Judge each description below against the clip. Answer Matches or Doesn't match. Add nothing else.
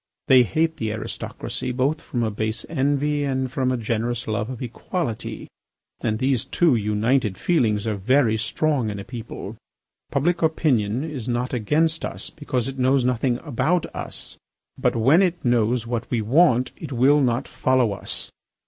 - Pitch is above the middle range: Doesn't match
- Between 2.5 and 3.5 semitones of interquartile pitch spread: Doesn't match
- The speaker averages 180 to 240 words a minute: Doesn't match